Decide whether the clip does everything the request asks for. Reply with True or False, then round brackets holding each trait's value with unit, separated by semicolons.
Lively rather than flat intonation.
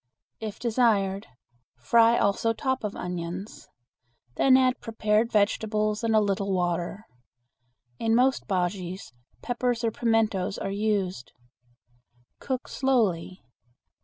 False (3.2 semitones)